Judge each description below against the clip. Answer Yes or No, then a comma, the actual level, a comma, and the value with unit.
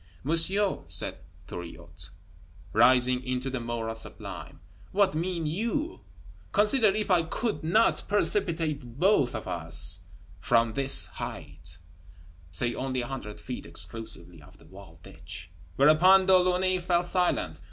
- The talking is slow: Yes, slow, 130 wpm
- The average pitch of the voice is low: No, medium, 145 Hz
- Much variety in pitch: Yes, wide, 8.0 semitones